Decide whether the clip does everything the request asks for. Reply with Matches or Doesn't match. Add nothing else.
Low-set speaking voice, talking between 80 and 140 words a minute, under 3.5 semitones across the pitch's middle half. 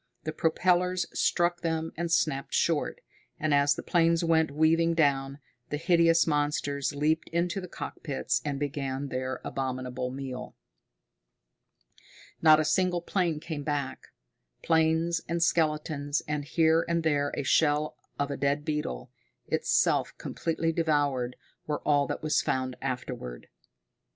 Doesn't match